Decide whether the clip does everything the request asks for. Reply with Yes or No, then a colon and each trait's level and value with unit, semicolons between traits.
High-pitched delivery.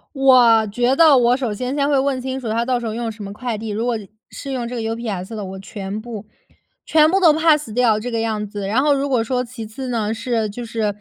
Yes: high, 235 Hz